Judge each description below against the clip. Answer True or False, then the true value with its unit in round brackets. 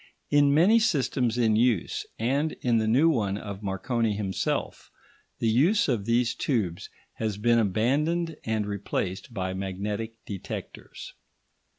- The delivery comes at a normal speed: False (130 wpm)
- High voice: False (115 Hz)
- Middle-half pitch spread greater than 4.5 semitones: True (4.9 semitones)